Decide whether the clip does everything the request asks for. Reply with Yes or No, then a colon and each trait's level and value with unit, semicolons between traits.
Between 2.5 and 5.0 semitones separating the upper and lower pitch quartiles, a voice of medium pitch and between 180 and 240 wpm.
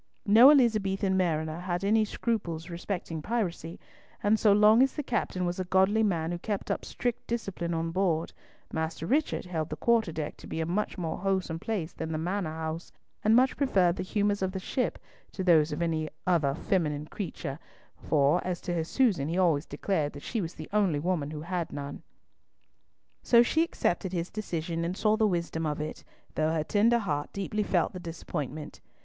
Yes: average, 4.3 semitones; medium, 180 Hz; average, 190 wpm